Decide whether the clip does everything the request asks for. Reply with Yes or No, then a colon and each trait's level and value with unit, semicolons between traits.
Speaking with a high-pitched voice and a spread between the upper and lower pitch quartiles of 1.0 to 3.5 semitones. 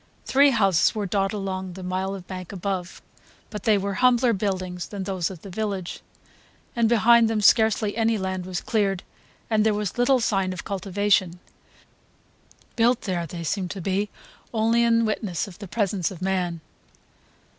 Yes: high, 195 Hz; average, 3.0 semitones